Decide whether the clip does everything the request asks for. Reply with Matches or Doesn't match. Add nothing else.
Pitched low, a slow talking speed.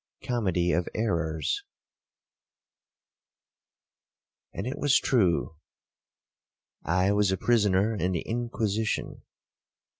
Matches